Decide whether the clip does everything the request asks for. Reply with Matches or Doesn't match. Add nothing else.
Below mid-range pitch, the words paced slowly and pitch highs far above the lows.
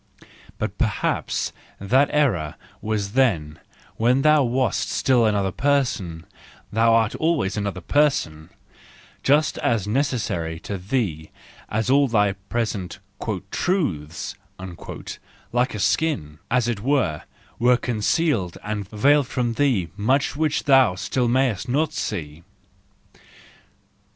Matches